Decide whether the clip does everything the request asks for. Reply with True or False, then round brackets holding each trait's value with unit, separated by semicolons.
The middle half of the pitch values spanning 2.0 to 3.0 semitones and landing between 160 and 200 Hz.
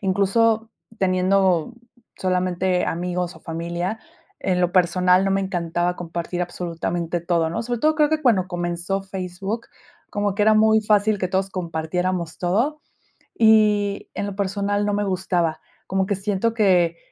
True (2.7 semitones; 190 Hz)